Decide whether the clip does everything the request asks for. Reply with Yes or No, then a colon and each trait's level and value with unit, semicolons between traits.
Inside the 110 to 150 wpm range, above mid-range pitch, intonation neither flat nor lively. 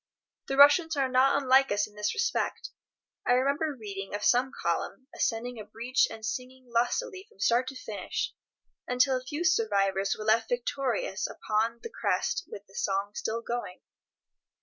No: average, 165 wpm; high, 245 Hz; average, 4.2 semitones